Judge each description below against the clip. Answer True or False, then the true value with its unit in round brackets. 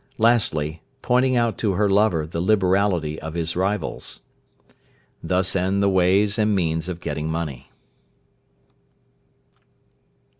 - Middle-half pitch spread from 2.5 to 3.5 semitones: False (4.2 semitones)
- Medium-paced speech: False (115 wpm)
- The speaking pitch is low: True (95 Hz)